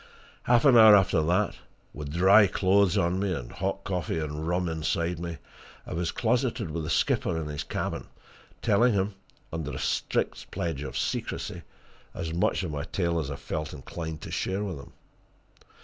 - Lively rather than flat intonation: No, average, 3.8 semitones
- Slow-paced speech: No, average, 180 wpm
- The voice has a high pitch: No, very low, 85 Hz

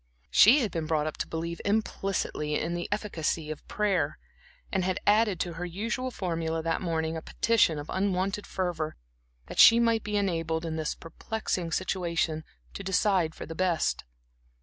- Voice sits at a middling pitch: Yes, medium, 175 Hz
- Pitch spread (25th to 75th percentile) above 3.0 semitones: Yes, average, 3.8 semitones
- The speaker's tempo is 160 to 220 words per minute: Yes, average, 170 wpm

